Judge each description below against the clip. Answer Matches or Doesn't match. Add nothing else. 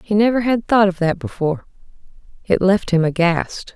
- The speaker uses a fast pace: Doesn't match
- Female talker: Matches